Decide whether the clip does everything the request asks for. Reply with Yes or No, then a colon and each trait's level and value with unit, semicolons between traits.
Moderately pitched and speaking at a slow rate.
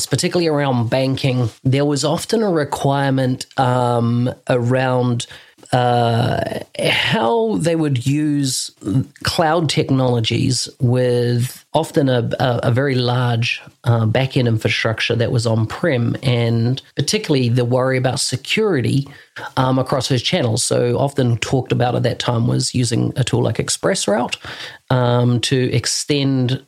No: low, 130 Hz; slow, 130 wpm